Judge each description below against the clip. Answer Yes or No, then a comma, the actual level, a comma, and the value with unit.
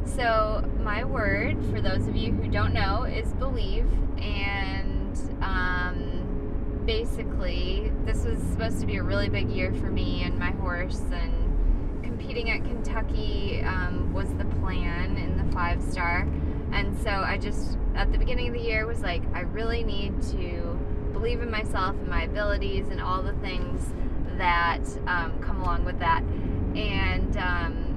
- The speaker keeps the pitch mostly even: Yes, narrow, 1.8 semitones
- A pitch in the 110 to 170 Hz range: No, very low, 90 Hz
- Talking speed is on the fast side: No, average, 160 wpm